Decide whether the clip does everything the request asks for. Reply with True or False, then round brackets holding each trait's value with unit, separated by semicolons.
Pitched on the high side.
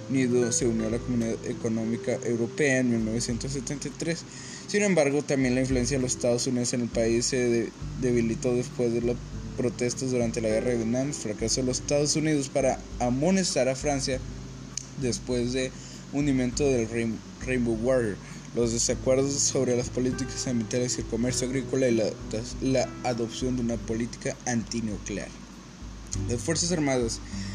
False (125 Hz)